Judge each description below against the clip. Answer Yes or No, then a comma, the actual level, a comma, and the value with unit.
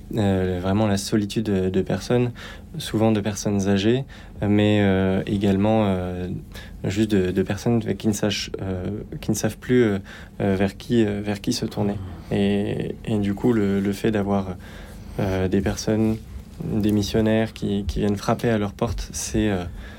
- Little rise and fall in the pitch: Yes, narrow, 2.0 semitones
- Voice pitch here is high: No, low, 100 Hz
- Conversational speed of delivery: Yes, average, 175 wpm